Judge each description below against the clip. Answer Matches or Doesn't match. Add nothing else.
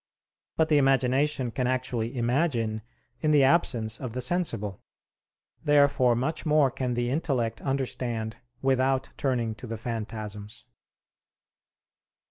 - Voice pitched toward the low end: Matches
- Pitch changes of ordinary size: Matches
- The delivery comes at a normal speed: Doesn't match